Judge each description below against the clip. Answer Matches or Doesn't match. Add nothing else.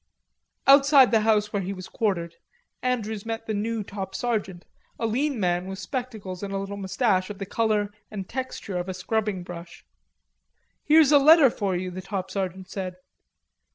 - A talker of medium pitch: Doesn't match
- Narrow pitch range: Doesn't match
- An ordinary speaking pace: Matches